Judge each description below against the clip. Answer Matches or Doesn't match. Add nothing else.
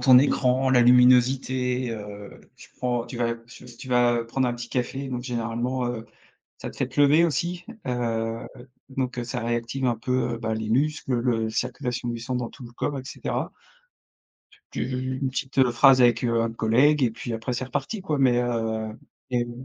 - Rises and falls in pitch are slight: Matches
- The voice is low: Matches